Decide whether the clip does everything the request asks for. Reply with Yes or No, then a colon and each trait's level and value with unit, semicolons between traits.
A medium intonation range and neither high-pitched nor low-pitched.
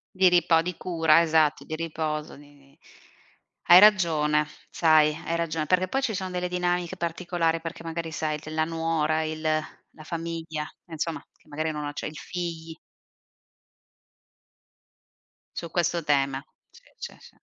No: narrow, 1.9 semitones; medium, 165 Hz